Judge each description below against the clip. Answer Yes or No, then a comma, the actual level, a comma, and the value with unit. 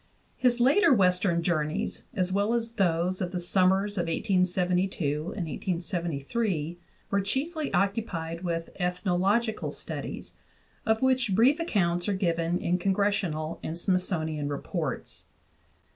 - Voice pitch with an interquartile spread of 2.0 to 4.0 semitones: Yes, average, 3.3 semitones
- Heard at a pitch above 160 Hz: Yes, medium, 185 Hz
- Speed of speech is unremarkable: No, slow, 125 wpm